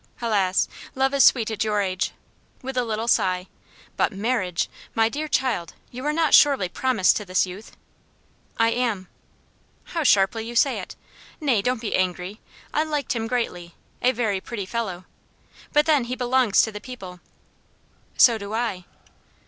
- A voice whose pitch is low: No, high, 225 Hz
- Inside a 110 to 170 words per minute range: Yes, average, 165 wpm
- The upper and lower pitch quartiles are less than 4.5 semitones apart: No, average, 4.8 semitones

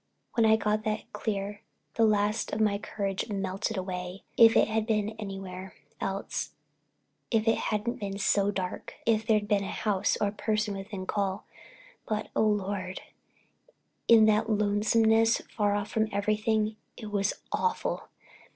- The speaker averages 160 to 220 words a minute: No, average, 150 wpm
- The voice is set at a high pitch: Yes, high, 210 Hz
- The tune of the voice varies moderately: No, narrow, 1.7 semitones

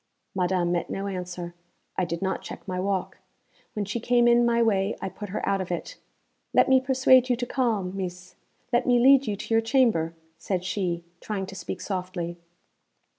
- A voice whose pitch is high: Yes, high, 195 Hz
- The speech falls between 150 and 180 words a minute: No, average, 190 wpm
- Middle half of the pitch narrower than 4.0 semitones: No, average, 4.6 semitones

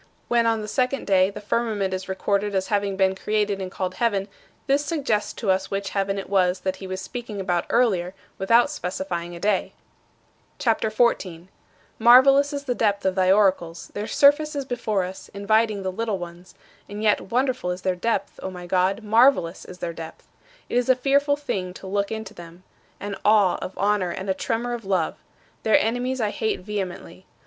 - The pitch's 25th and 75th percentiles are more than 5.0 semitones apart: No, average, 3.6 semitones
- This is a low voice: No, high, 200 Hz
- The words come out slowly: No, average, 195 wpm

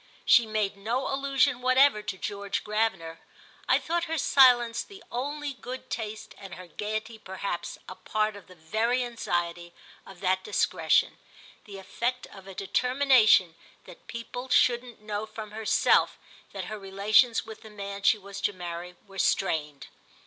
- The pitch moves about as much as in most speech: Yes, average, 4.1 semitones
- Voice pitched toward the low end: No, high, 215 Hz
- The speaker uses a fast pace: No, average, 150 wpm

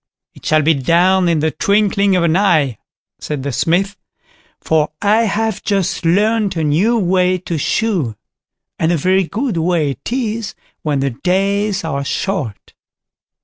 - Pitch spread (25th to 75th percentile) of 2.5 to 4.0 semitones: No, average, 4.4 semitones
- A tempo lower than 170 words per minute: Yes, average, 155 wpm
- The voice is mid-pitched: Yes, medium, 180 Hz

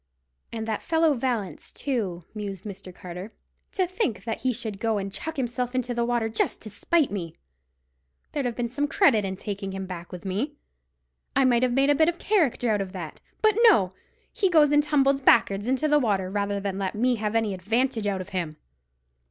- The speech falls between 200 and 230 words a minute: Yes, fast, 205 wpm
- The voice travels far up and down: Yes, wide, 5.7 semitones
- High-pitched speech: Yes, high, 225 Hz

